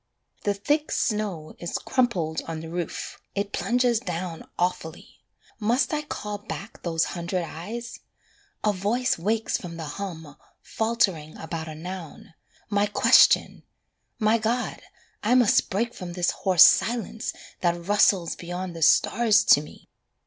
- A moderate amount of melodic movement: Yes, average, 4.9 semitones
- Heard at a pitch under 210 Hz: Yes, high, 190 Hz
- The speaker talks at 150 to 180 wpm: No, average, 140 wpm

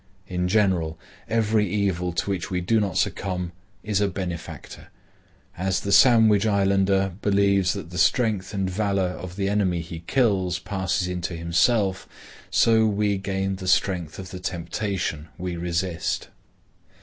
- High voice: No, very low, 95 Hz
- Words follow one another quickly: No, average, 145 wpm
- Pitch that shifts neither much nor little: No, narrow, 2.3 semitones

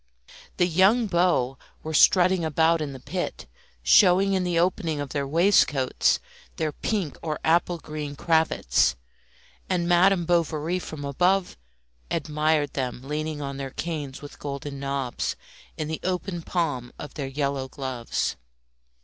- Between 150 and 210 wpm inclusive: No, slow, 135 wpm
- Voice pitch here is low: No, medium, 155 Hz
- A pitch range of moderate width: Yes, average, 4.0 semitones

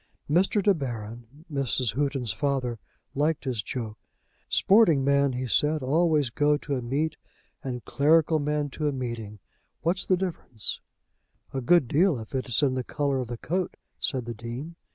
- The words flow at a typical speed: Yes, average, 170 wpm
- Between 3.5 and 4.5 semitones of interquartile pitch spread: Yes, average, 3.9 semitones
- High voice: No, medium, 140 Hz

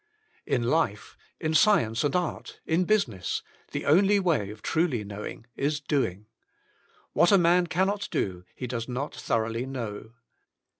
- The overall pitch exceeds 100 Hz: Yes, low, 135 Hz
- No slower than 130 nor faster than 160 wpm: Yes, average, 150 wpm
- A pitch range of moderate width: No, wide, 7.7 semitones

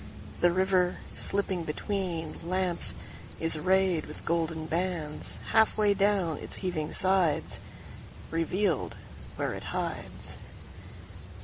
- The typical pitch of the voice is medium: Yes, medium, 180 Hz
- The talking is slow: Yes, slow, 90 wpm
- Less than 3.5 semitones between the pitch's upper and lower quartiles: Yes, average, 2.7 semitones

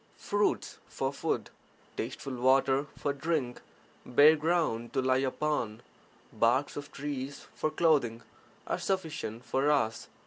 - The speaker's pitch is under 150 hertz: Yes, medium, 140 Hz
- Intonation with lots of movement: No, average, 3.5 semitones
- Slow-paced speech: Yes, slow, 125 wpm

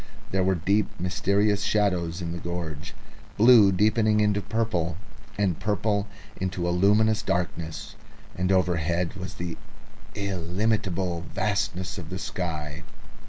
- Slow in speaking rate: Yes, slow, 120 wpm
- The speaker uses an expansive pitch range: No, average, 2.9 semitones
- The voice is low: Yes, very low, 95 Hz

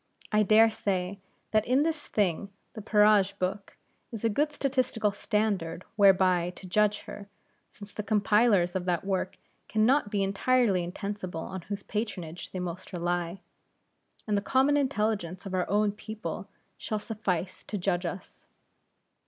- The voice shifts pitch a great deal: No, average, 2.9 semitones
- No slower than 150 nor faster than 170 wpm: Yes, average, 155 wpm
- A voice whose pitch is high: Yes, high, 205 Hz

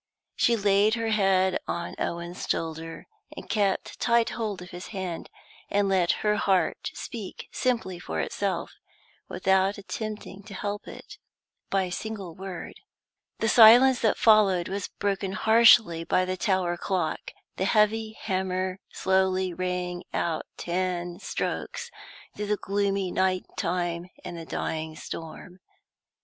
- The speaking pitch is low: No, high, 190 Hz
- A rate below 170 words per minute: Yes, slow, 135 wpm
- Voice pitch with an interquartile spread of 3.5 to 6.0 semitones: No, average, 2.8 semitones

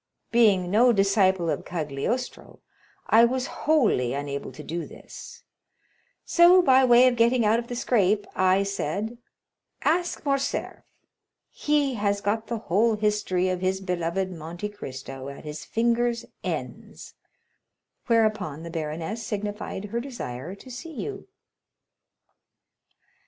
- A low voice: No, high, 210 Hz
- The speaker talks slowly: Yes, slow, 125 wpm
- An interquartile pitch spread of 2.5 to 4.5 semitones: No, average, 5.2 semitones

